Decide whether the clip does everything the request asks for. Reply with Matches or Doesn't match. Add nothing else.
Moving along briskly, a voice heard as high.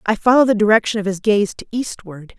Matches